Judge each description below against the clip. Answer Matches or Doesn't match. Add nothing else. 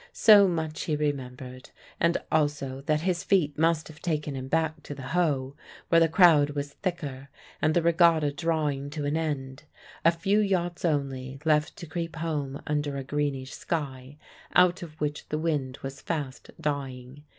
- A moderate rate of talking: Matches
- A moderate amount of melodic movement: Matches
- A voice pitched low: Doesn't match